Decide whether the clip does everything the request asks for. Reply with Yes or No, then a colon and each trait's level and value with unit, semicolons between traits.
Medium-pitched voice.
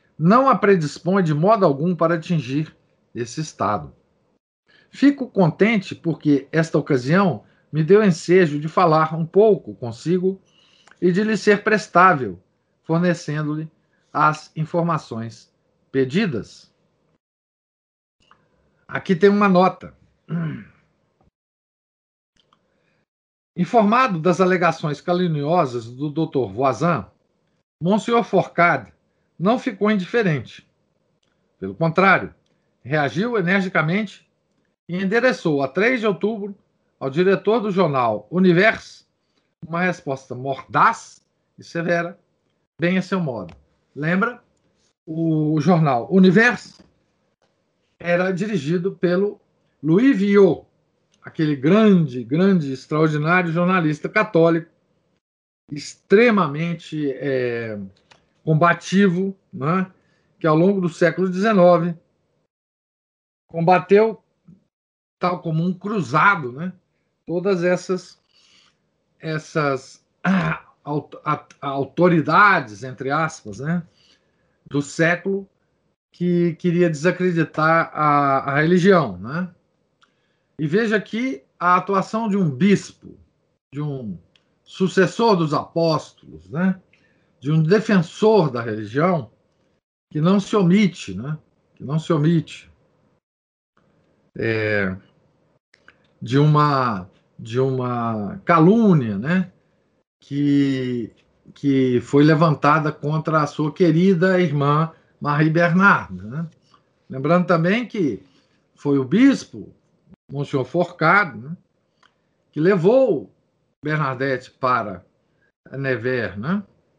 Yes: medium, 170 Hz